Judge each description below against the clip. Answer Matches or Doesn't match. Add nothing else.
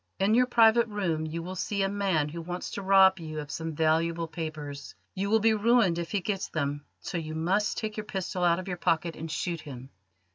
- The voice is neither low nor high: Matches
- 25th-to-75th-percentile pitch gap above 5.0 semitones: Doesn't match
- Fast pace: Matches